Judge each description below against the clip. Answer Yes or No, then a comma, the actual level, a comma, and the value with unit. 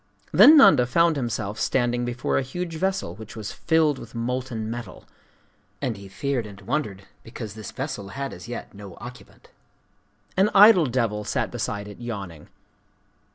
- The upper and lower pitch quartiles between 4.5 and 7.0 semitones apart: Yes, average, 4.8 semitones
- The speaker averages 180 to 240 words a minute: No, average, 155 wpm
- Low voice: Yes, low, 120 Hz